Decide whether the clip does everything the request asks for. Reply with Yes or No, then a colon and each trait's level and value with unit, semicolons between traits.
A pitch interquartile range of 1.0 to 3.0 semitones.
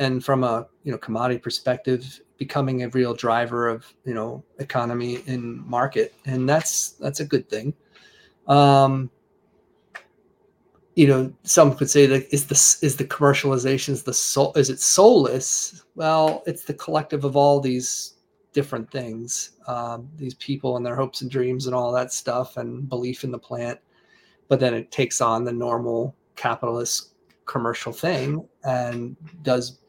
Yes: narrow, 2.5 semitones